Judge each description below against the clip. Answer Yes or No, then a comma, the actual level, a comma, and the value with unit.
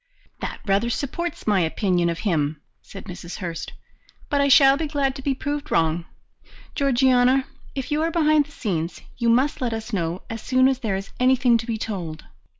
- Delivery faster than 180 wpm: Yes, average, 190 wpm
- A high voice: Yes, high, 240 Hz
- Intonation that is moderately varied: No, wide, 6.7 semitones